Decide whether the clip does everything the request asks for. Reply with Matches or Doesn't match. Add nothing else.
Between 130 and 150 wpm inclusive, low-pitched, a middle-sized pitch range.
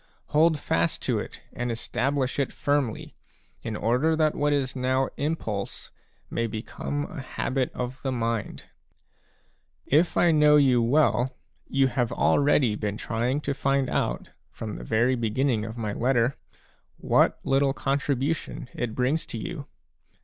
Matches